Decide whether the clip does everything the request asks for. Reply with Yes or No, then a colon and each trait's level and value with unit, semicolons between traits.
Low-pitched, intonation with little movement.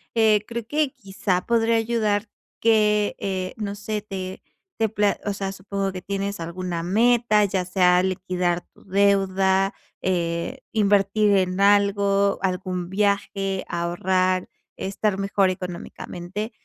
No: high, 195 Hz; narrow, 2.1 semitones